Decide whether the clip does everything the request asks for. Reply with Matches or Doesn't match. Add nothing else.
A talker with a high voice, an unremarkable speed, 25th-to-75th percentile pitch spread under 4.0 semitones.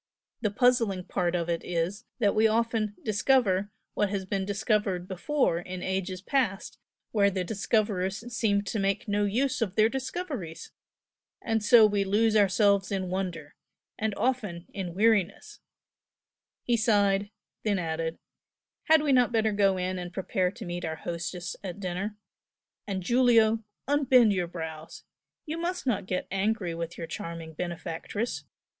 Matches